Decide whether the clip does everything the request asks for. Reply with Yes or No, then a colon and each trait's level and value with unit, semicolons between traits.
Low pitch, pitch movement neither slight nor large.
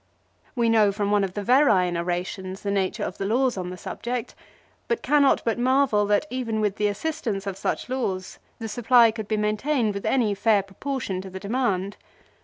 No: high, 210 Hz; average, 4.0 semitones